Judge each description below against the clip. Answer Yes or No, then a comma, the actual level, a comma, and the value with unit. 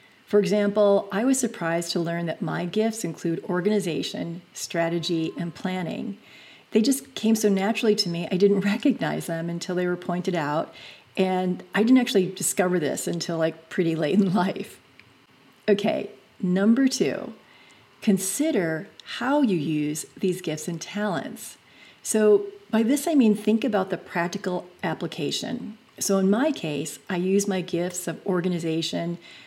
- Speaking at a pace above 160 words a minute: No, average, 150 wpm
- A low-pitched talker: No, high, 190 Hz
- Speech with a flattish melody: No, average, 3.8 semitones